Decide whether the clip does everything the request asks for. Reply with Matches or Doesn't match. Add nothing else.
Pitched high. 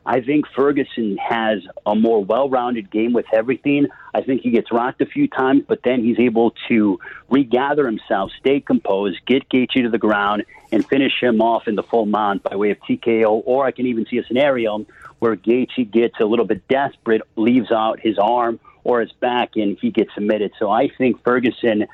Doesn't match